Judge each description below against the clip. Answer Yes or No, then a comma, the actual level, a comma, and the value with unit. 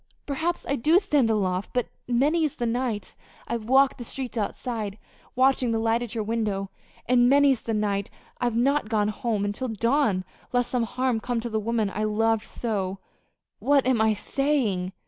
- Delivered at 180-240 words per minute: Yes, average, 185 wpm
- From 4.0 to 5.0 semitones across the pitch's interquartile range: No, average, 3.4 semitones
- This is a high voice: Yes, high, 235 Hz